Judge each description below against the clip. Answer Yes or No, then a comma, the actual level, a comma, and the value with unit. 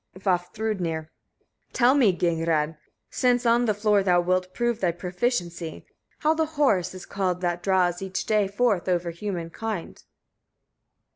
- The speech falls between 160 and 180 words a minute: No, average, 145 wpm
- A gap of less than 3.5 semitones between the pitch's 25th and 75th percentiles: No, average, 4.1 semitones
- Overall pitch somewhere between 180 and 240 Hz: Yes, medium, 185 Hz